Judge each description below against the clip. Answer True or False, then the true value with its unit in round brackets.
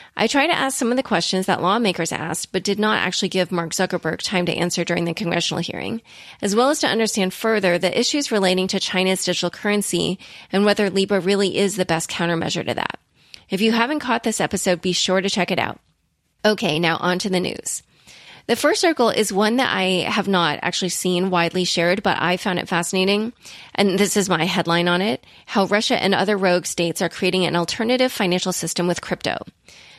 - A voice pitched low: False (185 Hz)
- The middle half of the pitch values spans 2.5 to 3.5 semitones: True (2.9 semitones)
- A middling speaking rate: False (210 wpm)